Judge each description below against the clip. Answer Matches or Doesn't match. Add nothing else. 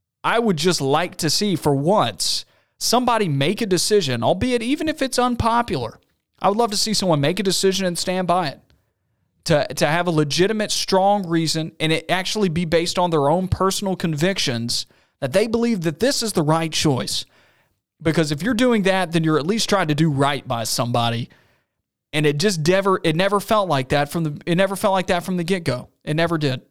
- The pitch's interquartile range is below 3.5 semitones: Doesn't match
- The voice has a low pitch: Doesn't match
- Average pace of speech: Doesn't match